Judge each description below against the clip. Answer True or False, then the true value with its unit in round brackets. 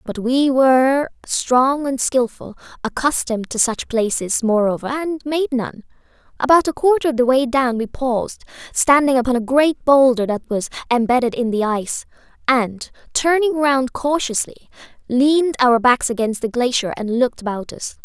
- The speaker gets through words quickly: False (160 wpm)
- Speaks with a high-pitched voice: True (255 Hz)